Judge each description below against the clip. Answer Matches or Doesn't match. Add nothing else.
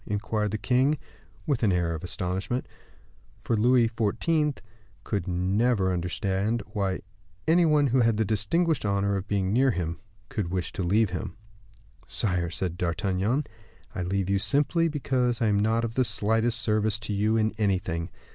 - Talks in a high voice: Doesn't match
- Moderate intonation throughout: Matches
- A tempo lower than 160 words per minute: Doesn't match